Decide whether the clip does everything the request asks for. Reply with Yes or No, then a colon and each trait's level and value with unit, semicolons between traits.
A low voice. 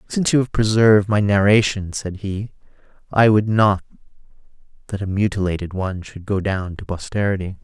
Yes: low, 100 Hz